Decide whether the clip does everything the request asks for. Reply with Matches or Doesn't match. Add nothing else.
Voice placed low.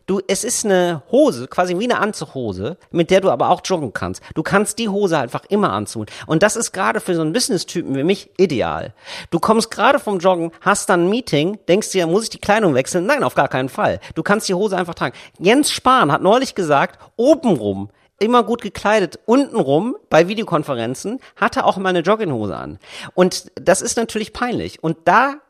Doesn't match